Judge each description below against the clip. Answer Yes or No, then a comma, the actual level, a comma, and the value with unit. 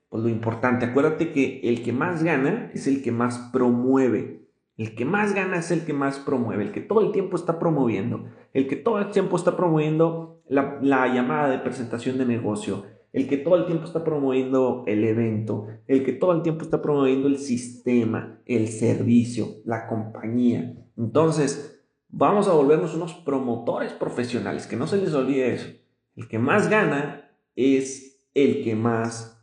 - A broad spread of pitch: No, average, 4.6 semitones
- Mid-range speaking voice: No, low, 130 Hz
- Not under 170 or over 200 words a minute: Yes, average, 175 wpm